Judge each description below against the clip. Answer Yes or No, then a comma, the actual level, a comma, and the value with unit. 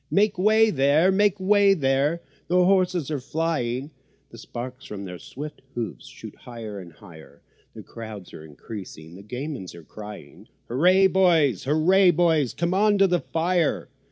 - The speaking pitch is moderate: Yes, medium, 150 Hz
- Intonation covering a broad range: Yes, wide, 8.4 semitones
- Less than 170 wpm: Yes, average, 155 wpm